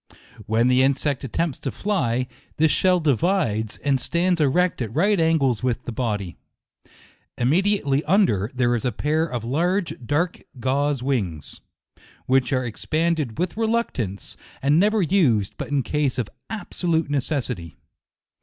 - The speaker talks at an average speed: Yes, average, 145 wpm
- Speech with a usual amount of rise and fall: No, wide, 5.7 semitones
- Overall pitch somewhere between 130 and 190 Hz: Yes, medium, 140 Hz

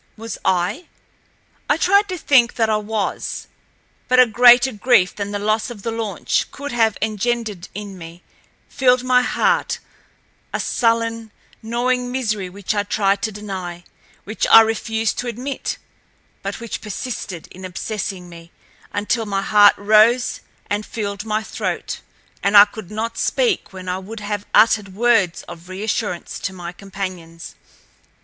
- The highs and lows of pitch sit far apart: No, average, 3.2 semitones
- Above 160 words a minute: No, average, 145 wpm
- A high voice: Yes, high, 215 Hz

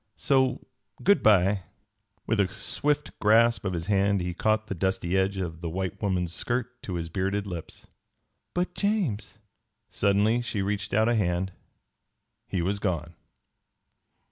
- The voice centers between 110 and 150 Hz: No, low, 100 Hz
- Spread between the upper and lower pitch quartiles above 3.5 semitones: No, average, 3.1 semitones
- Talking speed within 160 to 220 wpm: No, average, 150 wpm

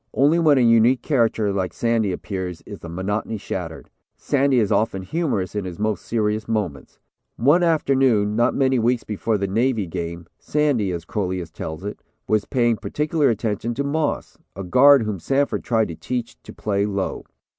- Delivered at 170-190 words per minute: Yes, average, 175 wpm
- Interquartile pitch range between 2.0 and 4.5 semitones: No, average, 5.1 semitones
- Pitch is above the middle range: No, low, 110 Hz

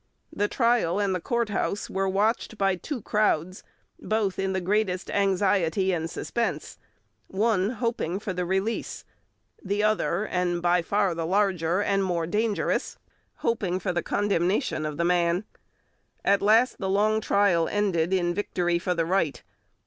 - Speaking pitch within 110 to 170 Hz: No, high, 195 Hz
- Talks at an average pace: Yes, average, 150 wpm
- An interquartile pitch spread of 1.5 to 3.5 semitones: Yes, average, 3.0 semitones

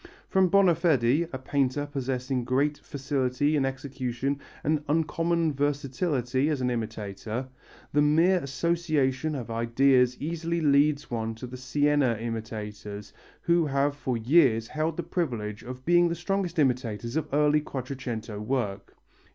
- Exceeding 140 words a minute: No, slow, 135 wpm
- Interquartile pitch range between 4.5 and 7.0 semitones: No, average, 3.9 semitones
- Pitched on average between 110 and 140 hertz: Yes, low, 135 Hz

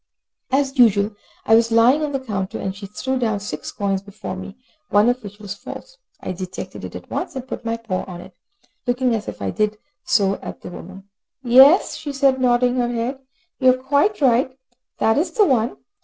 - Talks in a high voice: Yes, high, 235 Hz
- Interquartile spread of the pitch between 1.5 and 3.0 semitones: No, average, 4.4 semitones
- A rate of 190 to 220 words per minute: Yes, average, 200 wpm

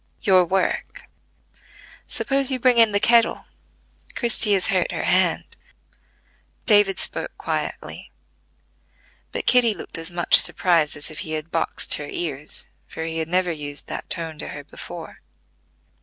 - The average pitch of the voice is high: No, medium, 175 Hz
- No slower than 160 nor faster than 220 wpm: No, average, 145 wpm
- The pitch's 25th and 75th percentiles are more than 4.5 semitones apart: Yes, average, 5.2 semitones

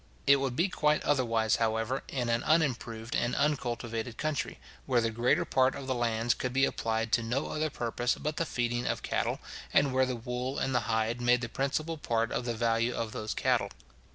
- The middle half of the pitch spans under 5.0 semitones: Yes, average, 2.7 semitones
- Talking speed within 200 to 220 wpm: Yes, fast, 205 wpm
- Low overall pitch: Yes, low, 120 Hz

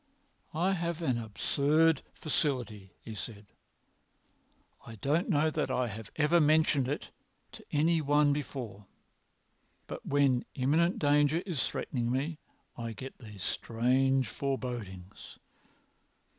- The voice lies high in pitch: No, medium, 140 Hz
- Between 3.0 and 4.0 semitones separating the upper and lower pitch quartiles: No, average, 4.6 semitones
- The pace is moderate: No, slow, 115 wpm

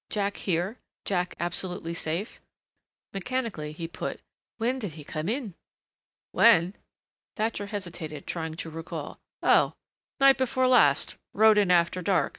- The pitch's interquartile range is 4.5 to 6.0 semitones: Yes, average, 5.0 semitones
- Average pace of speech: No, slow, 130 wpm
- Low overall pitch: No, medium, 185 Hz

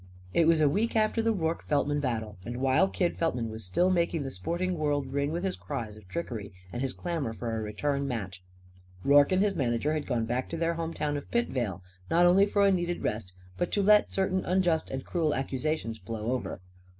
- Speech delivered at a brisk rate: Yes, fast, 215 wpm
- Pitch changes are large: Yes, wide, 6.6 semitones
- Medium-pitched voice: Yes, medium, 145 Hz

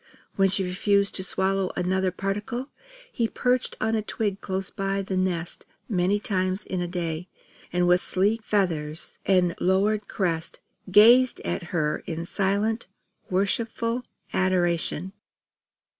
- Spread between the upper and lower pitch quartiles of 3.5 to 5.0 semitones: No, narrow, 2.5 semitones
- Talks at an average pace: No, slow, 130 wpm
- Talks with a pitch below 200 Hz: Yes, high, 190 Hz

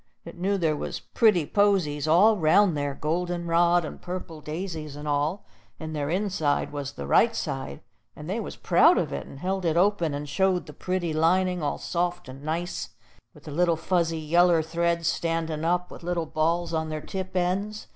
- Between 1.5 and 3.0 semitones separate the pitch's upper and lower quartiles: Yes, average, 2.7 semitones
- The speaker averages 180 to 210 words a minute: Yes, average, 190 wpm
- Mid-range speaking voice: Yes, medium, 170 Hz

